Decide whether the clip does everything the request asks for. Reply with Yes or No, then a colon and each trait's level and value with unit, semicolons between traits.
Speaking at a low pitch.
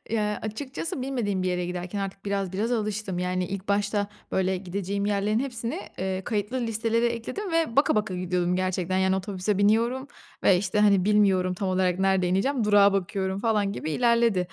No: high, 200 Hz